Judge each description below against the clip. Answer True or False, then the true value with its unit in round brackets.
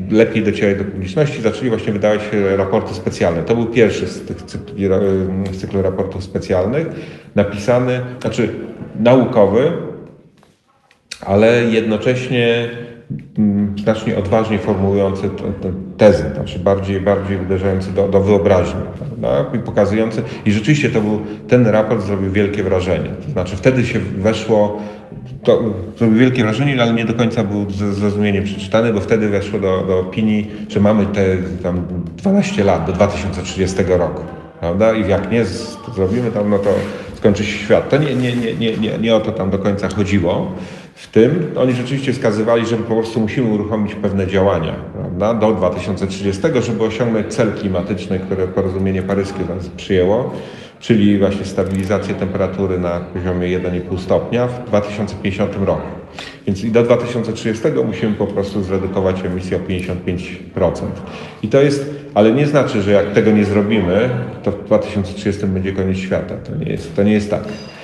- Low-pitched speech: True (105 Hz)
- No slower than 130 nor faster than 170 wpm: True (155 wpm)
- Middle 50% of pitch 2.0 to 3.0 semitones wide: True (2.6 semitones)